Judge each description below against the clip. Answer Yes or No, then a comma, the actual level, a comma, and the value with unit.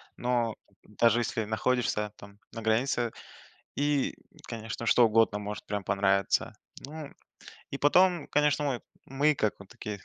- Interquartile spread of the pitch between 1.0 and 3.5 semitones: No, average, 4.7 semitones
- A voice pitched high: No, low, 115 Hz